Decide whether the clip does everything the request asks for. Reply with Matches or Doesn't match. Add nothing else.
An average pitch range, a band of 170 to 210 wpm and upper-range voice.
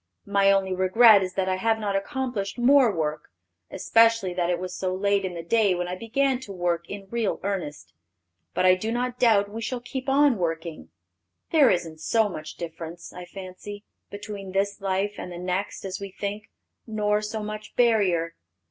Matches